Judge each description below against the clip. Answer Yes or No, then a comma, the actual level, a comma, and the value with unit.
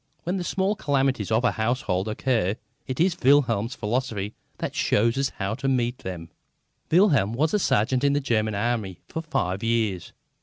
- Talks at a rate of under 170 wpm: No, average, 175 wpm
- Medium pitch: No, low, 120 Hz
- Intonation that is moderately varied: Yes, average, 4.8 semitones